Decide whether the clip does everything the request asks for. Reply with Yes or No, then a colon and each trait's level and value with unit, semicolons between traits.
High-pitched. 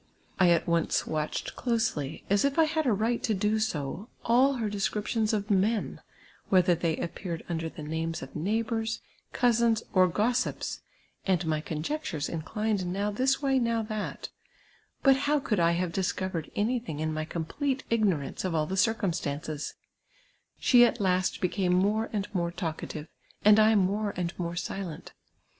Yes: high, 200 Hz